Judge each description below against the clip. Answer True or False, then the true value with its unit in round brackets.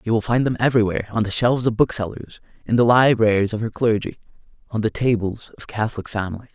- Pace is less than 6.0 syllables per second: False (6.6 syllables/s)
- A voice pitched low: True (110 Hz)